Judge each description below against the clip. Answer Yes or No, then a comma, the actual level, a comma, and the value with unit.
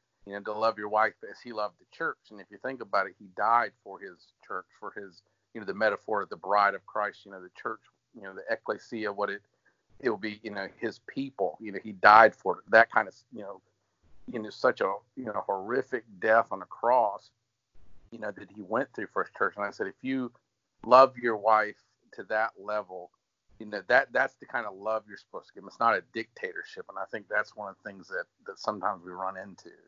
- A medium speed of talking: No, fast, 245 wpm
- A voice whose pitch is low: Yes, low, 110 Hz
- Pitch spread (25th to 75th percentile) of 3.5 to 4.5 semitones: Yes, average, 4.2 semitones